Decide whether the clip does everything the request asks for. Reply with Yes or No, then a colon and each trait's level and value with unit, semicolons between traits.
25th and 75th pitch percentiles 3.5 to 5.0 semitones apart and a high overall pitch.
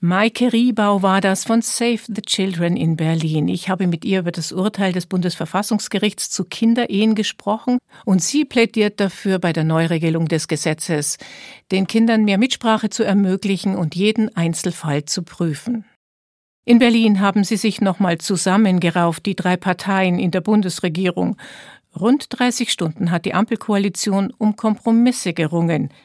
Yes: average, 3.9 semitones; high, 195 Hz